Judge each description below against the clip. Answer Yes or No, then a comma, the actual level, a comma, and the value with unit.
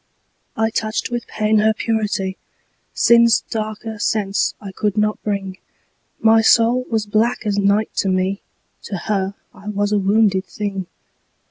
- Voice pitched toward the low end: No, high, 210 Hz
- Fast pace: No, average, 145 wpm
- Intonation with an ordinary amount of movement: No, narrow, 1.9 semitones